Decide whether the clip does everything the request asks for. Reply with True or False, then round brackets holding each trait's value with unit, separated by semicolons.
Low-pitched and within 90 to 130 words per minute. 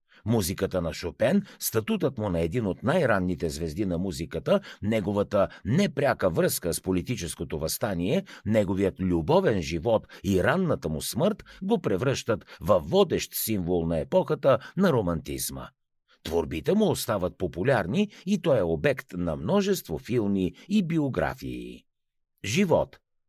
True (95 Hz; 125 wpm)